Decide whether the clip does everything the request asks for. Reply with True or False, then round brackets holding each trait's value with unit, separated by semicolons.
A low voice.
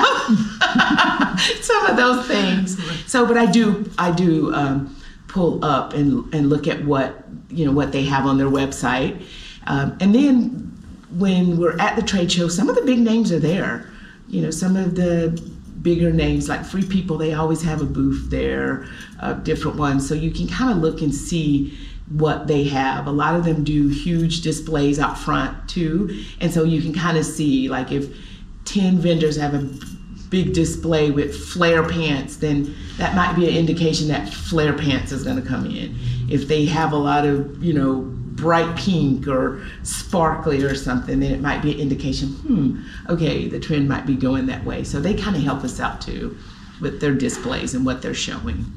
False (155 Hz)